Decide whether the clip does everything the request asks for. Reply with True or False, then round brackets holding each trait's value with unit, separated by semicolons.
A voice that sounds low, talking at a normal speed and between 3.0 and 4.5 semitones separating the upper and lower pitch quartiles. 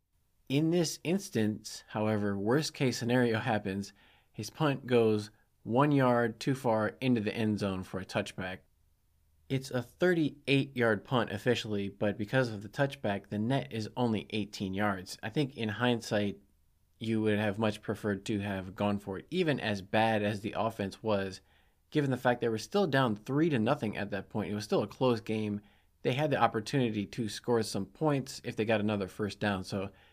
True (110 Hz; 185 wpm; 3.6 semitones)